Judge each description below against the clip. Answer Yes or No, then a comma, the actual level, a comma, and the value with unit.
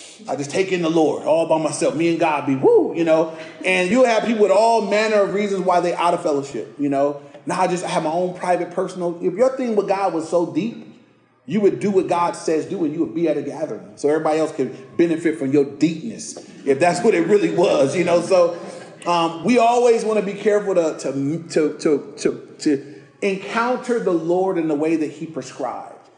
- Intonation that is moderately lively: Yes, average, 4.1 semitones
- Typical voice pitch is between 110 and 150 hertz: No, medium, 175 Hz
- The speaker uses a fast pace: Yes, fast, 230 wpm